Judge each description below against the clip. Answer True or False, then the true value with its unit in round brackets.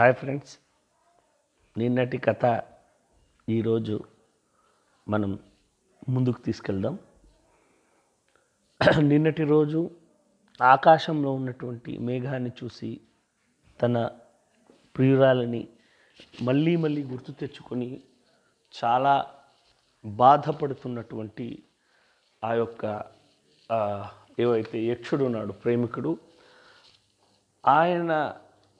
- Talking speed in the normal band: False (60 wpm)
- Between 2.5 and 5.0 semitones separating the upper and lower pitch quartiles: True (4.0 semitones)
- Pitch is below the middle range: True (125 Hz)